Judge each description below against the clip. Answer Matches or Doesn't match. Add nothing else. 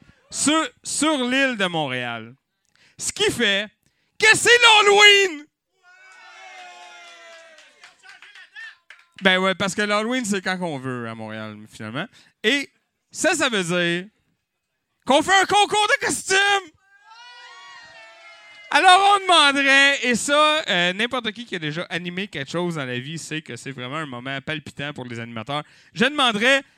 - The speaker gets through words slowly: Matches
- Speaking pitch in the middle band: Doesn't match